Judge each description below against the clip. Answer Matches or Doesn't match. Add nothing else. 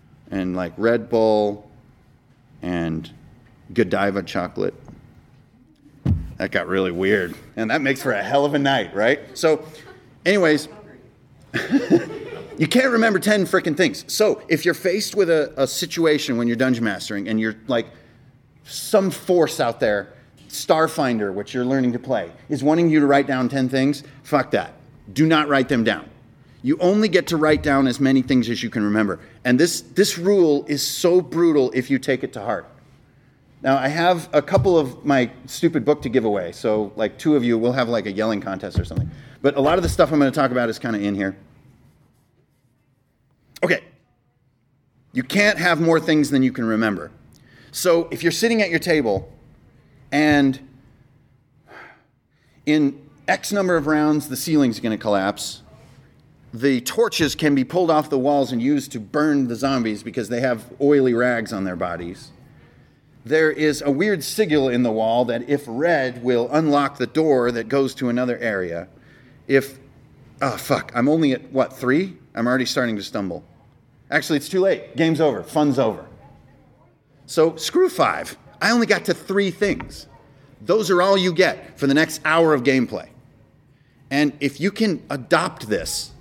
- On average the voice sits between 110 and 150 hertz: Matches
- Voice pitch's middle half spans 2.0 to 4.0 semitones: Doesn't match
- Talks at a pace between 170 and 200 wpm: Matches